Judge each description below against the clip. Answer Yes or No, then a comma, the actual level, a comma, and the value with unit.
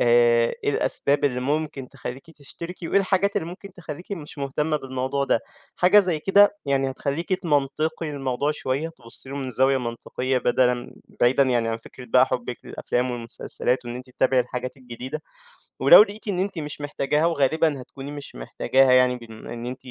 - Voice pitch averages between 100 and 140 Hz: Yes, low, 135 Hz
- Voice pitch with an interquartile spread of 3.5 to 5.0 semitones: Yes, average, 3.9 semitones